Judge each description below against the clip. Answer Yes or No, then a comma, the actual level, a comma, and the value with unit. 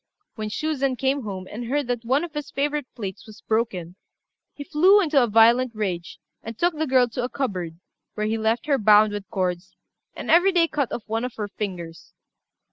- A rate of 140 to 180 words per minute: No, fast, 205 wpm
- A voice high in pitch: Yes, high, 230 Hz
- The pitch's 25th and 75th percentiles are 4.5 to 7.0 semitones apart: Yes, average, 5.3 semitones